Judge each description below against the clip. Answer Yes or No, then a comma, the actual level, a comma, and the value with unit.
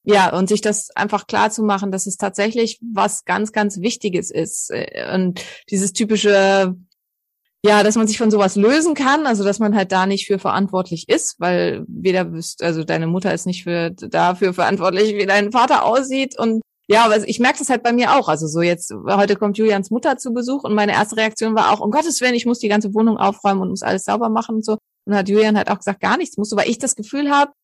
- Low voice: No, high, 210 Hz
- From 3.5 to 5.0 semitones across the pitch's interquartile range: No, average, 2.7 semitones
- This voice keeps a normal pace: No, fast, 225 wpm